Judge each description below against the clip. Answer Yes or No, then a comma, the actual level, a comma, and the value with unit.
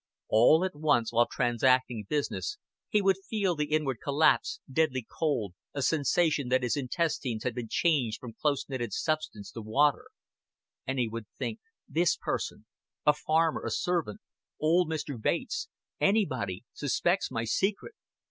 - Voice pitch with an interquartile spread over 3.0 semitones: Yes, average, 5.3 semitones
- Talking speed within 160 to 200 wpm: No, average, 150 wpm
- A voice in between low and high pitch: Yes, medium, 145 Hz